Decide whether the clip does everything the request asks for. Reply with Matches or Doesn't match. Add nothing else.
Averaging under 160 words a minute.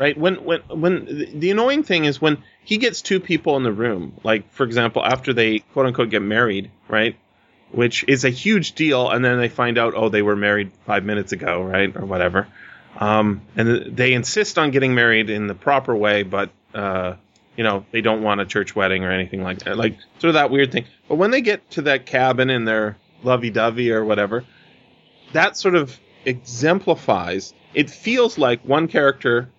Doesn't match